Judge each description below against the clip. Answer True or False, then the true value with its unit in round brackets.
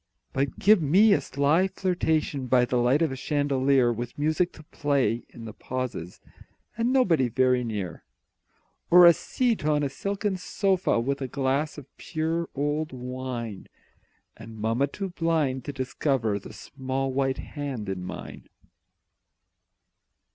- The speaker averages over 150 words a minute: False (145 wpm)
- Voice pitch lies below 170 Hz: True (140 Hz)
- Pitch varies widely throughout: False (4.2 semitones)